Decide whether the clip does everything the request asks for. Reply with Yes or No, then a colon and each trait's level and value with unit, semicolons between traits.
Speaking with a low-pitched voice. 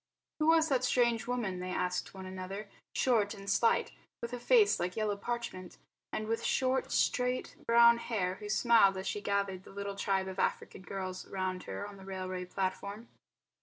No: high, 200 Hz